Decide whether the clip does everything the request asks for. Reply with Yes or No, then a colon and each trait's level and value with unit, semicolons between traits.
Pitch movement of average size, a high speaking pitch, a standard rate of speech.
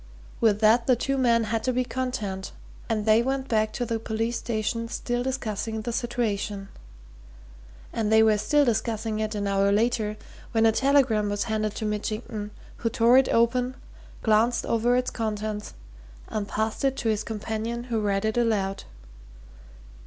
No: narrow, 2.1 semitones; high, 225 Hz; average, 165 wpm